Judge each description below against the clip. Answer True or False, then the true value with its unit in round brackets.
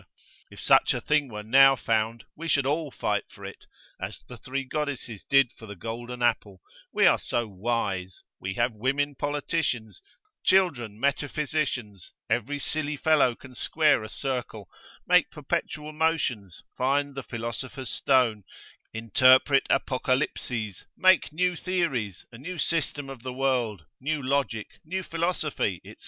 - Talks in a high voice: False (130 Hz)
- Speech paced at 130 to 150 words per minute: True (145 wpm)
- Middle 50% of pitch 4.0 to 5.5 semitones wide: True (4.5 semitones)